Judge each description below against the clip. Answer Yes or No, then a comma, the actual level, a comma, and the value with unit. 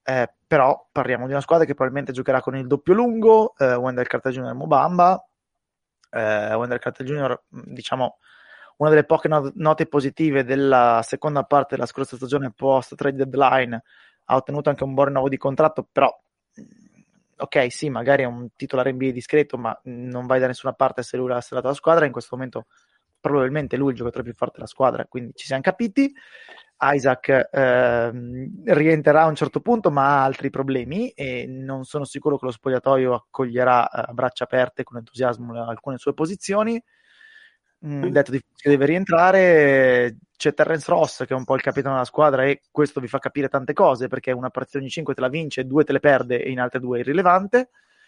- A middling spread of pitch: Yes, average, 3.0 semitones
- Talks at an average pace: No, fast, 190 wpm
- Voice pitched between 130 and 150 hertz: Yes, low, 135 Hz